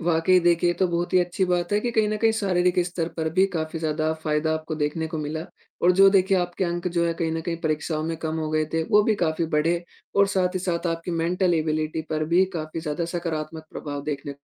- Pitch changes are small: Yes, narrow, 2.3 semitones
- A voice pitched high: No, medium, 170 Hz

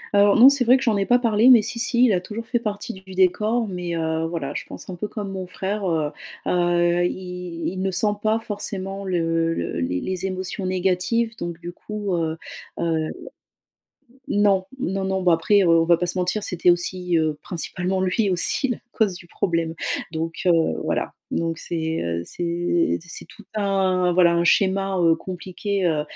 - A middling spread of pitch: Yes, average, 3.1 semitones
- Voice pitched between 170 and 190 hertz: Yes, medium, 185 Hz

